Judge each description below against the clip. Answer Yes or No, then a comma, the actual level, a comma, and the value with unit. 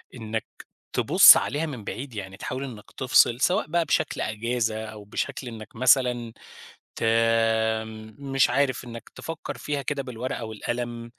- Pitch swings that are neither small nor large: Yes, average, 3.4 semitones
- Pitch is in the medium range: No, low, 120 Hz